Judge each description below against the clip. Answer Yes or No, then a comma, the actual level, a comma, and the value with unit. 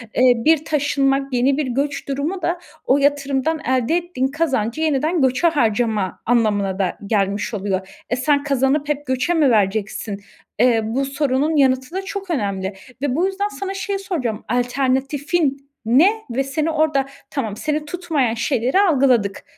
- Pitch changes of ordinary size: Yes, average, 4.4 semitones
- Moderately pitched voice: No, very high, 275 Hz